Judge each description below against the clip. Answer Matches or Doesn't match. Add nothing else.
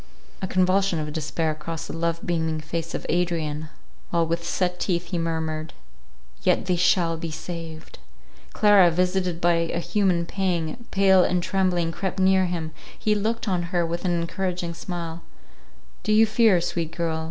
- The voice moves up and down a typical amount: Doesn't match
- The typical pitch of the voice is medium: Matches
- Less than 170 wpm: Matches